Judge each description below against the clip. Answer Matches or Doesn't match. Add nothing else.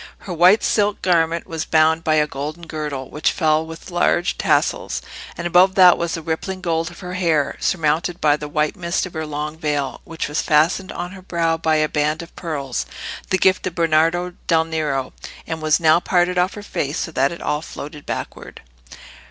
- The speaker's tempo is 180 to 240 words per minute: Matches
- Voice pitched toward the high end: Doesn't match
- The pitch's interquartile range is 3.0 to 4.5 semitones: Doesn't match